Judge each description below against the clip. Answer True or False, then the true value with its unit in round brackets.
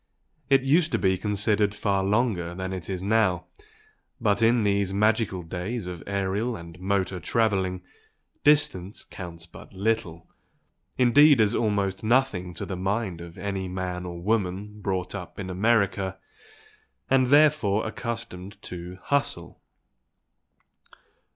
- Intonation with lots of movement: False (3.5 semitones)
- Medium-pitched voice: False (100 Hz)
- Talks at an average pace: False (130 wpm)